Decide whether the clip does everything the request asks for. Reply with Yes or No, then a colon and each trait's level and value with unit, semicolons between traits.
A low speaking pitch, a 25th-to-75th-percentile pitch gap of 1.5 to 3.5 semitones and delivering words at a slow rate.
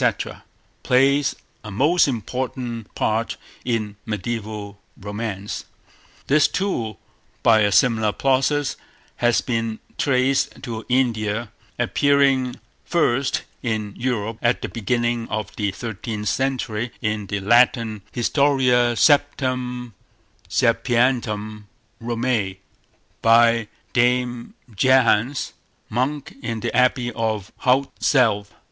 Yes: low, 120 Hz; average, 3.0 semitones; slow, 100 wpm